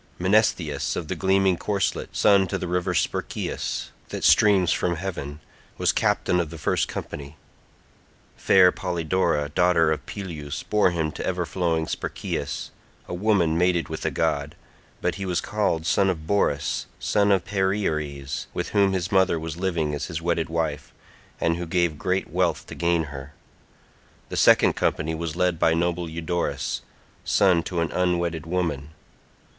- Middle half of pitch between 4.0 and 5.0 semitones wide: No, average, 2.8 semitones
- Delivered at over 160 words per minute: No, average, 155 wpm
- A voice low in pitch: Yes, very low, 85 Hz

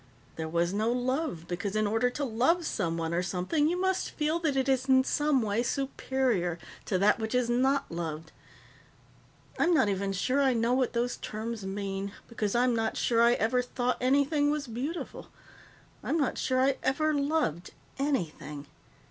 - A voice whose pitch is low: No, high, 245 Hz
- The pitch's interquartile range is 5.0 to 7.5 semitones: Yes, wide, 5.6 semitones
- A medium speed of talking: Yes, average, 175 wpm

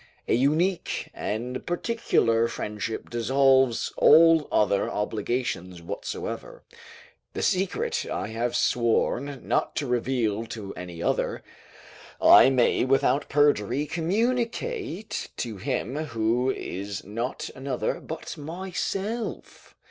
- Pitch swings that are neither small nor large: No, wide, 6.1 semitones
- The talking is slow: Yes, slow, 105 wpm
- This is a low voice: Yes, low, 130 Hz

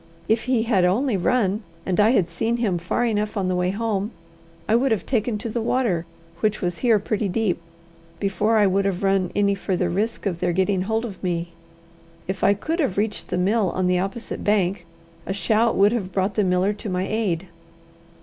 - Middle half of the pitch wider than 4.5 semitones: No, average, 3.2 semitones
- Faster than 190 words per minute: Yes, fast, 205 wpm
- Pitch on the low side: No, high, 200 Hz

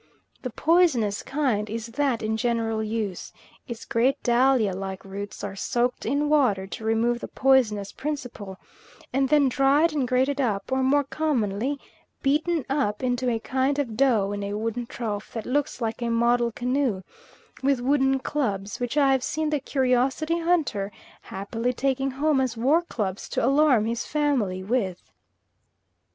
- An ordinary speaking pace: Yes, average, 160 wpm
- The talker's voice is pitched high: Yes, very high, 250 Hz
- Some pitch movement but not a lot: Yes, average, 4.0 semitones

